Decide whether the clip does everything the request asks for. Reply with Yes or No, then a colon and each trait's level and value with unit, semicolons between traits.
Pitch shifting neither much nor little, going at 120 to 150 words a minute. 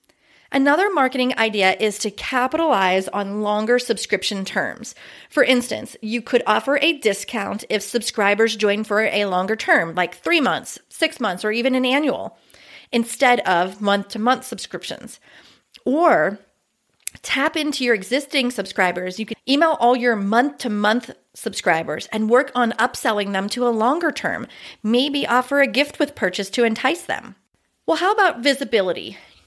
Yes: average, 4.2 semitones; average, 145 wpm